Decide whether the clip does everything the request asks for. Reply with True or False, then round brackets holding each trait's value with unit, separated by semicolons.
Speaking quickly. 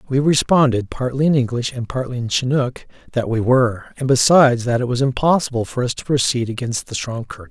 True (210 wpm)